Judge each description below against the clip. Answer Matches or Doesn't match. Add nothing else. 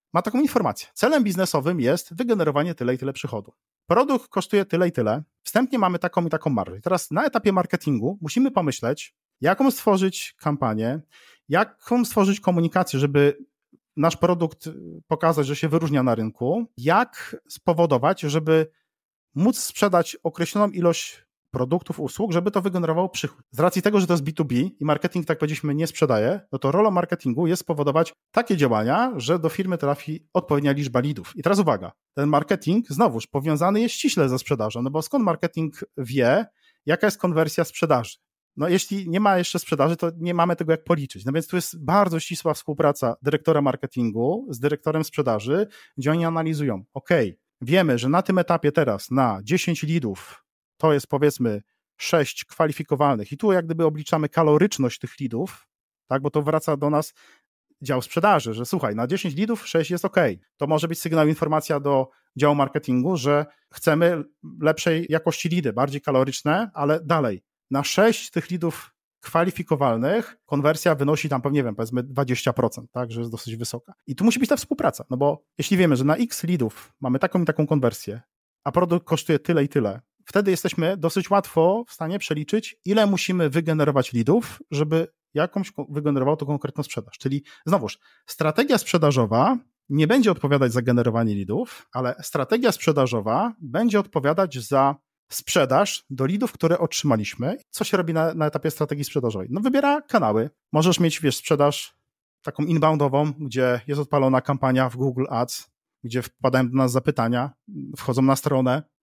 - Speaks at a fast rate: Matches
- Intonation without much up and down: Doesn't match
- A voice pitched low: Doesn't match